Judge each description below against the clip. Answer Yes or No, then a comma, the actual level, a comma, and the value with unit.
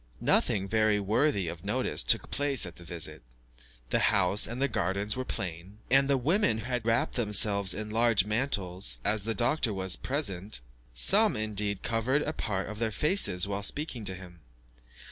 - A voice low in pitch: Yes, low, 105 Hz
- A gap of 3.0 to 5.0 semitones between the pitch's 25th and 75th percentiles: Yes, average, 4.2 semitones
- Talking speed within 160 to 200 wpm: Yes, average, 165 wpm